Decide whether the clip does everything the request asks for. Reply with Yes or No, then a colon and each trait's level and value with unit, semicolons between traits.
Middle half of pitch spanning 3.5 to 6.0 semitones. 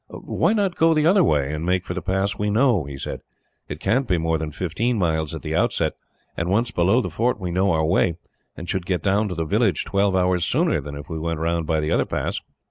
Yes: average, 4.5 semitones